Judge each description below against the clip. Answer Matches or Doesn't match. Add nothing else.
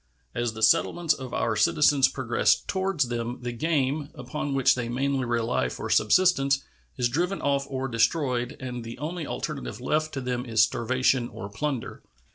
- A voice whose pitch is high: Doesn't match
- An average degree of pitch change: Matches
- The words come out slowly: Doesn't match